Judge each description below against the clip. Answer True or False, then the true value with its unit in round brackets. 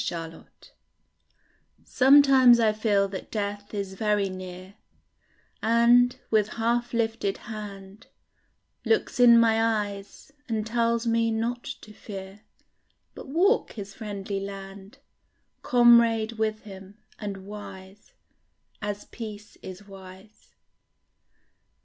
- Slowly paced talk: True (105 wpm)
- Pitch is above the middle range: True (215 Hz)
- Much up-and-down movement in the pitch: False (2.8 semitones)